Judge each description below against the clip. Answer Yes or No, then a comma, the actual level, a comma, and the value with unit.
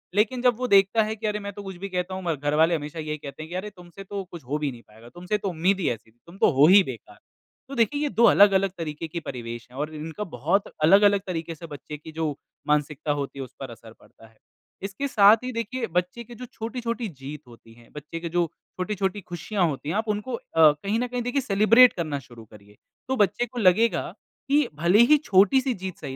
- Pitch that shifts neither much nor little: No, wide, 6.0 semitones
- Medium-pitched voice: Yes, medium, 180 Hz